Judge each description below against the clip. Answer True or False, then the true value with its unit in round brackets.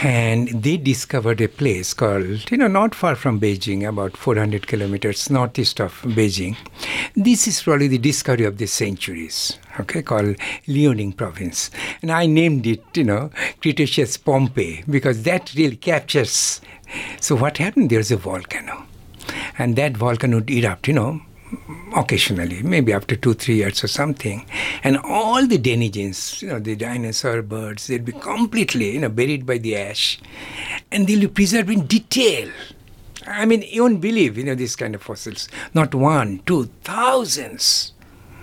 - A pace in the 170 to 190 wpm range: False (160 wpm)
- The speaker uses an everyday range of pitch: False (6.5 semitones)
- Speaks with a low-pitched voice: True (125 Hz)